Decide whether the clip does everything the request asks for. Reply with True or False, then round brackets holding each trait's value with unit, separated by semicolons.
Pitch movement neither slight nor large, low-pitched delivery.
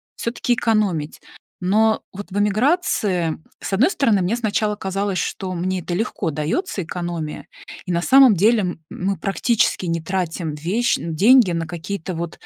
False (4.2 semitones; 190 Hz)